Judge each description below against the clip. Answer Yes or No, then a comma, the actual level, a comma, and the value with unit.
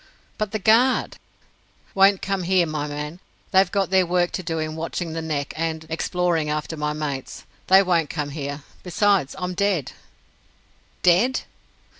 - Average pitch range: Yes, average, 3.8 semitones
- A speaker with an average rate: Yes, average, 155 wpm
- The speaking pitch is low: No, medium, 170 Hz